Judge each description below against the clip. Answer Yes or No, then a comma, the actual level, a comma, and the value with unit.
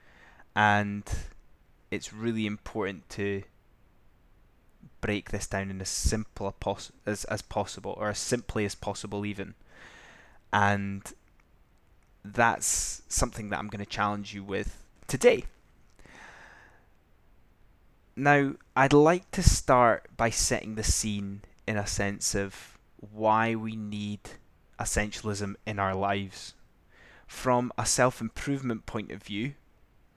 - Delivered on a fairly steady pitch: Yes, narrow, 2.0 semitones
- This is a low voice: Yes, low, 105 Hz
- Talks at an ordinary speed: No, slow, 115 wpm